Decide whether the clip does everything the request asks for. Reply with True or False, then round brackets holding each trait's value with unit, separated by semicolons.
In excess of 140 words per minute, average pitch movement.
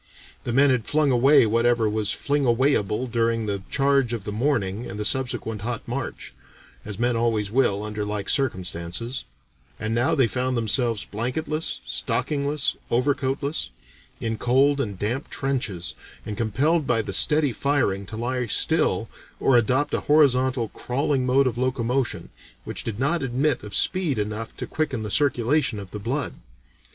True (160 wpm; 4.1 semitones)